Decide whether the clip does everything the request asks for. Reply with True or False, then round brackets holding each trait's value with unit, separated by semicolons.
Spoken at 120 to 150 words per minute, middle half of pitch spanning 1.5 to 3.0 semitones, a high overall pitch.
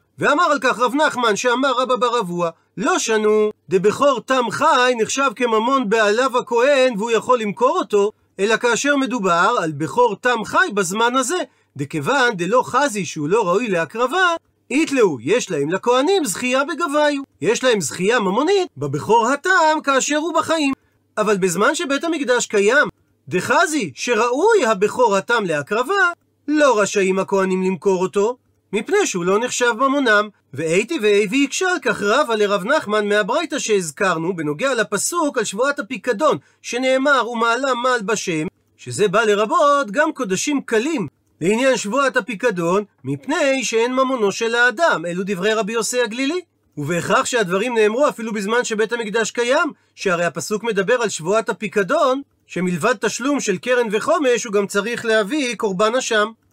False (145 wpm; 5.1 semitones; 235 Hz)